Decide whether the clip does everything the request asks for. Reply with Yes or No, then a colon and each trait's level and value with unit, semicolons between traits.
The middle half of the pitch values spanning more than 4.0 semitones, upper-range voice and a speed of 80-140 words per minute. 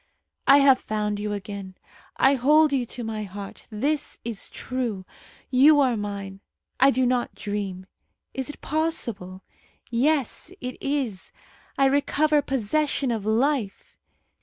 Yes: average, 5.1 semitones; high, 245 Hz; slow, 135 wpm